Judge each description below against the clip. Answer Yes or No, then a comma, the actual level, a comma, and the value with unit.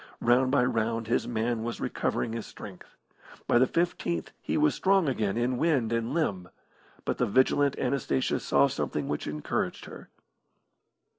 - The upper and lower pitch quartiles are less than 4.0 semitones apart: Yes, average, 3.6 semitones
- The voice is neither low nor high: No, low, 120 Hz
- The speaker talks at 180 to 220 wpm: No, average, 155 wpm